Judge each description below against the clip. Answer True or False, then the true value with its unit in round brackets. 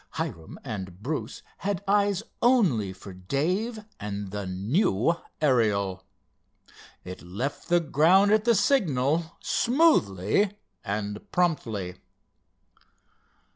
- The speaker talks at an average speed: False (95 wpm)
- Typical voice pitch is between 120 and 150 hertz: True (135 Hz)